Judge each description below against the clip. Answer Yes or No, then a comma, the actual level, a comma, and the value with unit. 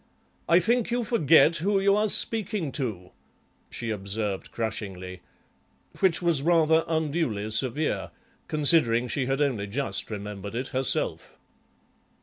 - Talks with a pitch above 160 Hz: No, medium, 140 Hz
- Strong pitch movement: Yes, wide, 7.7 semitones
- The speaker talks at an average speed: No, slow, 125 wpm